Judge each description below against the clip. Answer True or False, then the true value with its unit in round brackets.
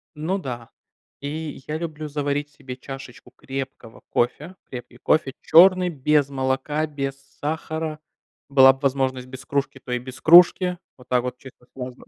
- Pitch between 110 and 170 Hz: True (140 Hz)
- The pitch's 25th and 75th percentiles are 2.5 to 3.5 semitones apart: True (3.0 semitones)